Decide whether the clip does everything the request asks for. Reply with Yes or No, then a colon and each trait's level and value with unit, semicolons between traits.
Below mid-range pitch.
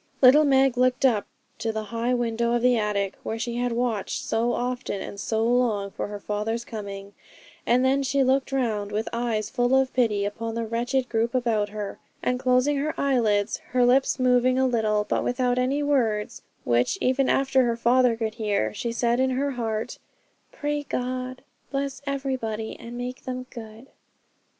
No: high, 240 Hz